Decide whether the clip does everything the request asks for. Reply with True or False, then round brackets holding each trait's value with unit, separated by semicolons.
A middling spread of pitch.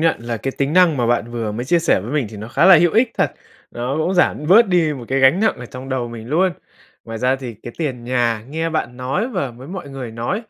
False (5.8 semitones)